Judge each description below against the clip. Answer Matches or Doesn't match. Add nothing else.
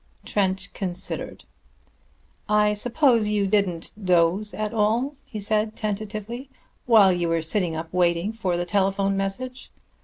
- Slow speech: Matches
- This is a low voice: Doesn't match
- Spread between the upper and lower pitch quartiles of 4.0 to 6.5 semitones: Doesn't match